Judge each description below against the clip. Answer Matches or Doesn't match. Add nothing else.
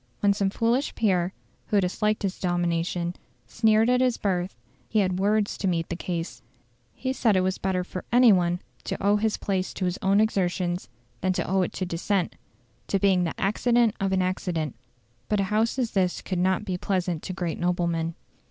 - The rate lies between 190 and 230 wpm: Matches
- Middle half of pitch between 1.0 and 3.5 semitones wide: Matches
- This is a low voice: Doesn't match